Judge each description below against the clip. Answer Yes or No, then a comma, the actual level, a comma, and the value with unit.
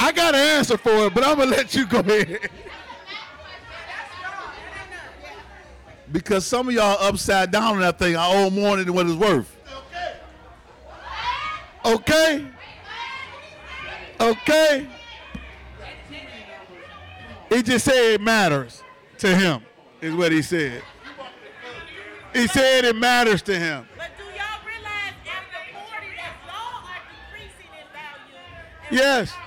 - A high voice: Yes, high, 235 Hz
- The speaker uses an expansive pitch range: Yes, wide, 8.0 semitones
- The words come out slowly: Yes, slow, 100 wpm